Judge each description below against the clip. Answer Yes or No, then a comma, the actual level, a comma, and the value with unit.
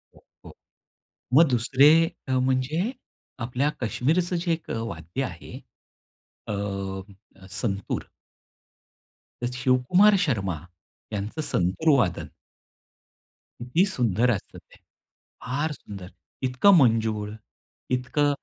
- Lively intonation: Yes, wide, 6.5 semitones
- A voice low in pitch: Yes, low, 125 Hz